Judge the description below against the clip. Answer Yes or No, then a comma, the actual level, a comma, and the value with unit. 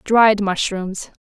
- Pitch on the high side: Yes, high, 200 Hz